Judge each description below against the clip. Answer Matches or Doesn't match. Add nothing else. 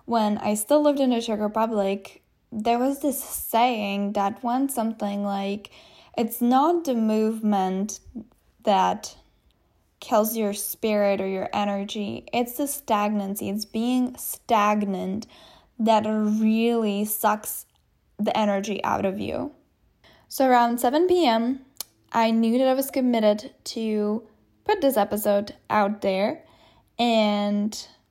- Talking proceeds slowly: Matches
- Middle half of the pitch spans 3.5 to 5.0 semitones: Doesn't match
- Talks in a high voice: Matches